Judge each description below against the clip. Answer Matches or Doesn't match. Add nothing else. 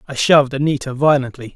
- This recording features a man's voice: Matches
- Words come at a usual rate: Matches